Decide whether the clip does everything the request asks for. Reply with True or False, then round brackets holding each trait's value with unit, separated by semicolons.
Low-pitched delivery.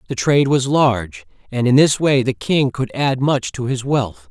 True (130 Hz)